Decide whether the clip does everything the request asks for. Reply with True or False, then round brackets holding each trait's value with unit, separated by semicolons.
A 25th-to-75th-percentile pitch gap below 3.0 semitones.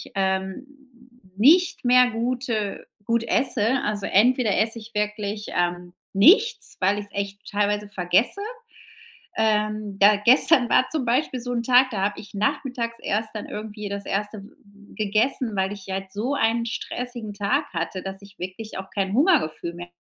False (3.6 semitones)